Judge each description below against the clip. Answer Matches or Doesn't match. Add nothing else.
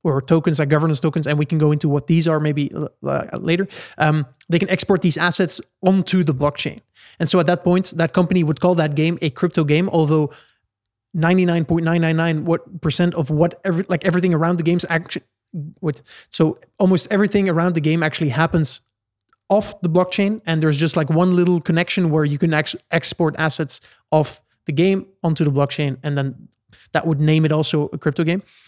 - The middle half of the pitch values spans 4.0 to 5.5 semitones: Doesn't match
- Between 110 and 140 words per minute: Doesn't match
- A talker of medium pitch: Matches